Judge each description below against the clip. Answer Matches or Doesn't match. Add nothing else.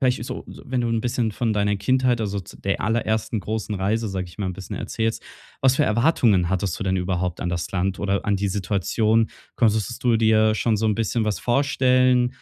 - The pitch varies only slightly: Doesn't match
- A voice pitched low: Matches